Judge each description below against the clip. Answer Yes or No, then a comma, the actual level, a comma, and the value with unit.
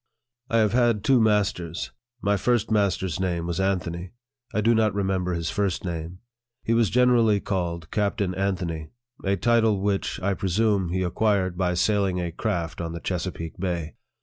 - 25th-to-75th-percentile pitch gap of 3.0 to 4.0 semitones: Yes, average, 3.4 semitones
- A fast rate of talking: No, average, 165 wpm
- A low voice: Yes, very low, 95 Hz